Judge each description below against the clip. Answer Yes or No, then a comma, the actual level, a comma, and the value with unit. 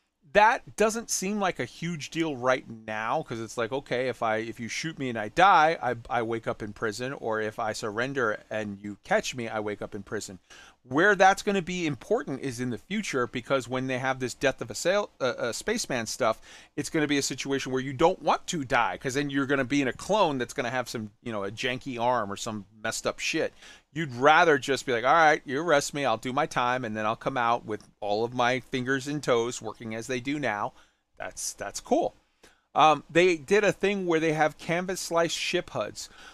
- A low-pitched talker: Yes, low, 130 Hz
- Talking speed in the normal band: No, fast, 240 wpm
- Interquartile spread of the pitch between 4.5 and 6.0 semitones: Yes, average, 4.8 semitones